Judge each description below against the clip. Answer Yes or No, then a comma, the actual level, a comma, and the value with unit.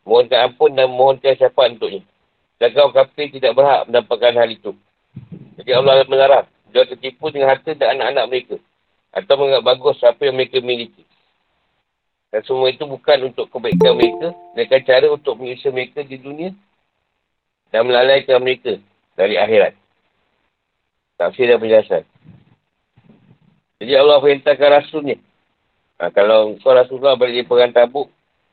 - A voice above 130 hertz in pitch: Yes, medium, 140 Hz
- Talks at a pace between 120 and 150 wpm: Yes, average, 145 wpm